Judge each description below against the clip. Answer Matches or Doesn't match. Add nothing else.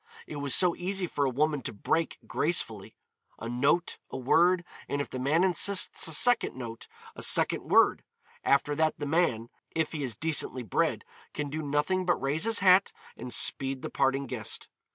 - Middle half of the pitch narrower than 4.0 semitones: Doesn't match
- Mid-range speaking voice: Matches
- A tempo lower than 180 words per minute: Doesn't match